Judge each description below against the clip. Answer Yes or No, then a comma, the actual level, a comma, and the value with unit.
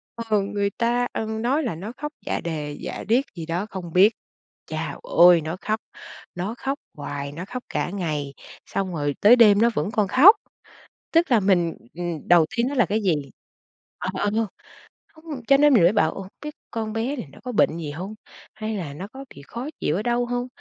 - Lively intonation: Yes, wide, 5.8 semitones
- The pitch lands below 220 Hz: Yes, high, 205 Hz